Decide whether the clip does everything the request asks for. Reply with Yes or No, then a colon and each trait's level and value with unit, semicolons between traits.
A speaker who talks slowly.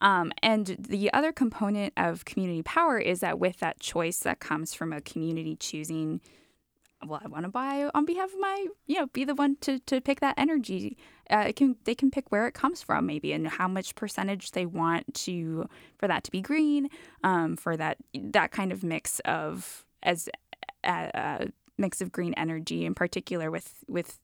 No: average, 200 wpm